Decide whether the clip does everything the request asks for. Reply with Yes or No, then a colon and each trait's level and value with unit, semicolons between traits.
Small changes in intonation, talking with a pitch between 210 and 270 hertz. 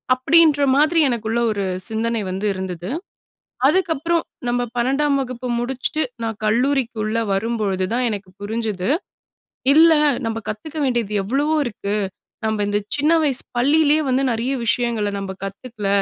No: average, 4.7 semitones; high, 235 Hz